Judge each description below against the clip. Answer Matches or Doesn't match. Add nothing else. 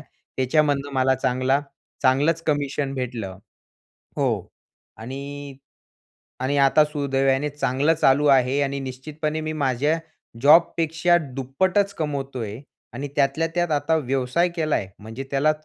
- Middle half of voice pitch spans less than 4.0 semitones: Matches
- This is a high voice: Doesn't match